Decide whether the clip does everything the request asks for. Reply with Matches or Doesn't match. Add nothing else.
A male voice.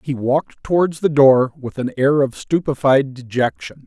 Matches